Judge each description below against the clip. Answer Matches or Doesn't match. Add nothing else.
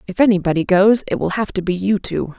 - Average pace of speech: Doesn't match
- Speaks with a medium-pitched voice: Doesn't match